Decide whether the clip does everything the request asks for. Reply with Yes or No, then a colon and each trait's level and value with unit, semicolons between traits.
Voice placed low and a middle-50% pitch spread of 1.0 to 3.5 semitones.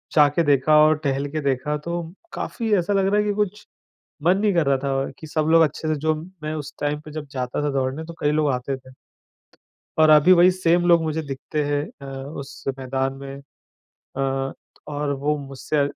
No: medium, 150 Hz; average, 3.2 semitones